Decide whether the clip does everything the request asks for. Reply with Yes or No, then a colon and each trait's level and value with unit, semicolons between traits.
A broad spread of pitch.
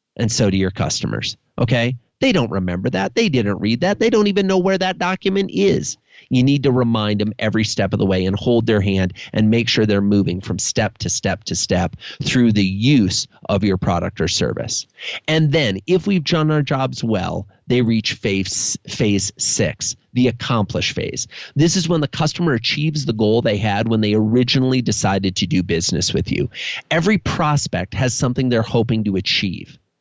Yes: wide, 6.2 semitones